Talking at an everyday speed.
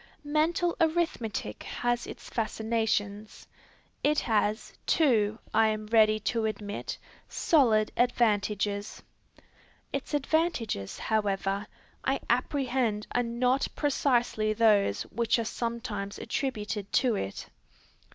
No: slow, 100 wpm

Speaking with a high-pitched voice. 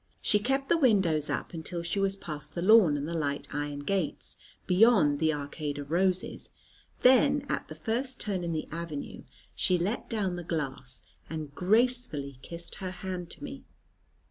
No: medium, 175 Hz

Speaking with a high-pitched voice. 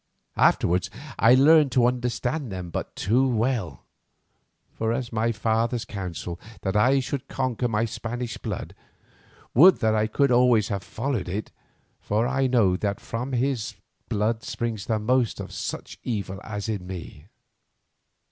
No: low, 115 Hz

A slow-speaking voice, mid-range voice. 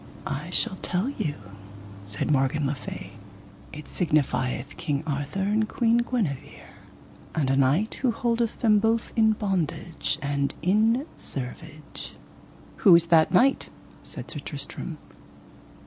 Yes: slow, 130 wpm; medium, 170 Hz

